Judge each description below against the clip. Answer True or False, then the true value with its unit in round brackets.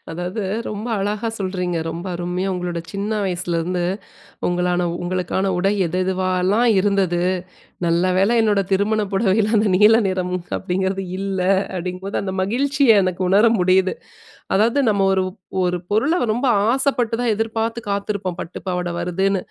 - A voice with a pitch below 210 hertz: True (190 Hz)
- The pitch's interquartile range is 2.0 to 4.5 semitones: True (2.8 semitones)